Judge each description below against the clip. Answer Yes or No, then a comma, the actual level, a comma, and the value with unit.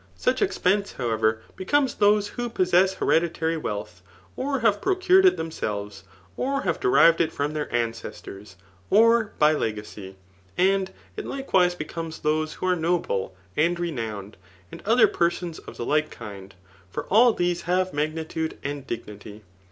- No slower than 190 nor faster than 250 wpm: No, average, 145 wpm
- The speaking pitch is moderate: Yes, medium, 165 Hz